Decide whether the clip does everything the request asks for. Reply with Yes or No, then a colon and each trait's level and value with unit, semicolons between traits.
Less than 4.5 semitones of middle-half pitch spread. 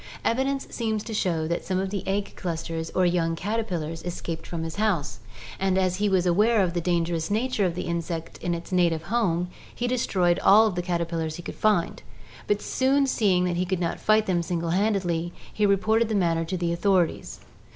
Yes: average, 3.6 semitones